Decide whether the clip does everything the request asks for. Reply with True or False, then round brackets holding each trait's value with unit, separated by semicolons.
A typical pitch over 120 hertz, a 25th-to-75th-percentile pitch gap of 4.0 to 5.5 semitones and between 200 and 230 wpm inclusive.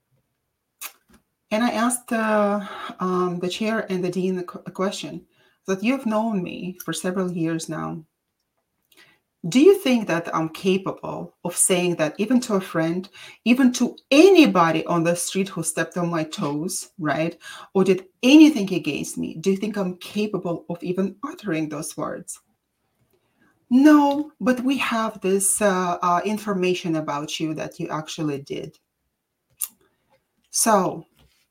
False (185 Hz; 4.6 semitones; 145 wpm)